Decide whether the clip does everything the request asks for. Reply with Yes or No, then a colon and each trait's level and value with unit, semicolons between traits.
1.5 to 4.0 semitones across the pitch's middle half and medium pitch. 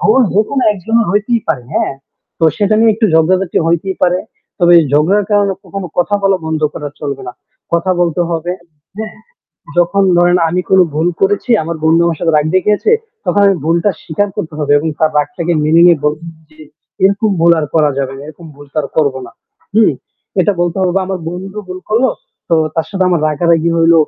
Yes: average, 3.6 semitones; medium, 175 Hz